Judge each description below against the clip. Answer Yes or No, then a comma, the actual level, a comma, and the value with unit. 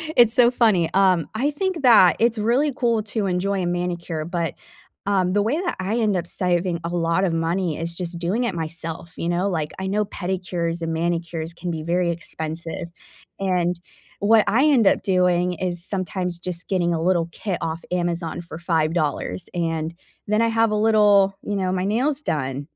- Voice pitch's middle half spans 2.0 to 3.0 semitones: No, average, 3.5 semitones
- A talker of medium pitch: Yes, medium, 180 Hz